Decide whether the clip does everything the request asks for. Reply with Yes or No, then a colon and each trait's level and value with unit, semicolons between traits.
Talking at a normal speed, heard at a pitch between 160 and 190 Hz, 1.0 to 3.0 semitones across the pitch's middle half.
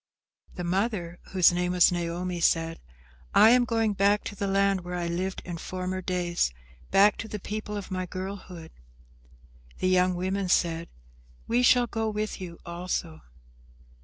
Yes: average, 160 wpm; medium, 185 Hz; narrow, 2.6 semitones